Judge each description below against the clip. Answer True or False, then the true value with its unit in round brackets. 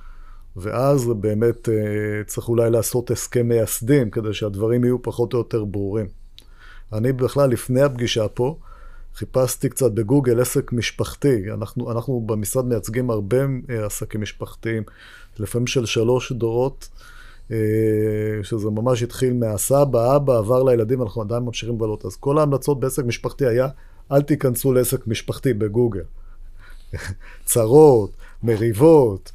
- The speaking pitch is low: True (115 Hz)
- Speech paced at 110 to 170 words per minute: True (120 wpm)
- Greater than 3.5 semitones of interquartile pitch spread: False (3.0 semitones)